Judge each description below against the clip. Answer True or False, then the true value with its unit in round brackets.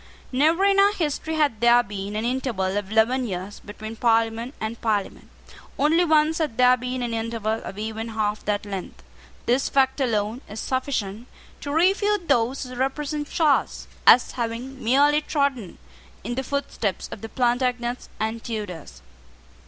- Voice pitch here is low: False (240 Hz)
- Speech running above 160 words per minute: False (155 wpm)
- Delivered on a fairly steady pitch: False (4.4 semitones)